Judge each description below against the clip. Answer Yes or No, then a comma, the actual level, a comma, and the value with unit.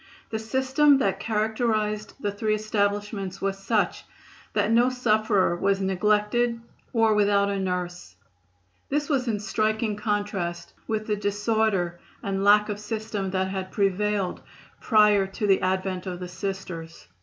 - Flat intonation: Yes, narrow, 2.1 semitones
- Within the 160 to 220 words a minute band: No, average, 140 wpm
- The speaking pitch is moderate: No, high, 205 Hz